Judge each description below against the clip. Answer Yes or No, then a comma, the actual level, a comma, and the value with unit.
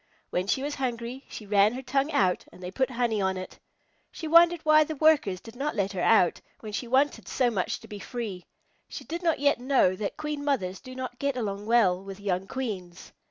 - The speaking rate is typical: No, fast, 220 wpm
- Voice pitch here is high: Yes, high, 240 Hz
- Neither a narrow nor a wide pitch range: No, wide, 6.1 semitones